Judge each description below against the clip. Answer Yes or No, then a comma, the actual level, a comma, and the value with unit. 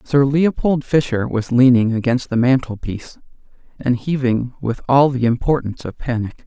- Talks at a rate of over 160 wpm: No, average, 150 wpm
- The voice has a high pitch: No, low, 125 Hz